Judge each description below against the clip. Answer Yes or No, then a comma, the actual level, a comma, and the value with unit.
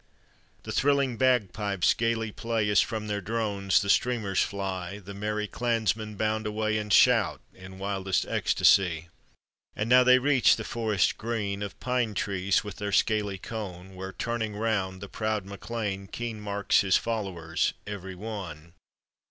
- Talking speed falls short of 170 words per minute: Yes, average, 150 wpm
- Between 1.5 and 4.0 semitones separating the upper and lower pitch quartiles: Yes, average, 2.7 semitones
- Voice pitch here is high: No, low, 105 Hz